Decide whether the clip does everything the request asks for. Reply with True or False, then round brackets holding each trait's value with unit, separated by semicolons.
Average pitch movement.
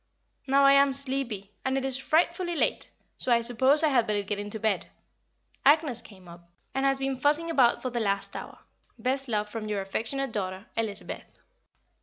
True (4.6 semitones)